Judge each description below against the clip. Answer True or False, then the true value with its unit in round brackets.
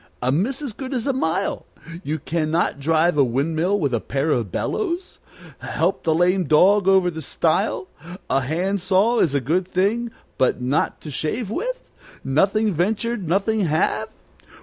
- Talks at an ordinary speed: True (170 wpm)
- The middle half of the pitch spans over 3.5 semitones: True (5.4 semitones)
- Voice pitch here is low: False (175 Hz)